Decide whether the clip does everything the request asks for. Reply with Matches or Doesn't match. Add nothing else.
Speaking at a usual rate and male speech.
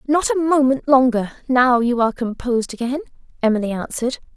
Doesn't match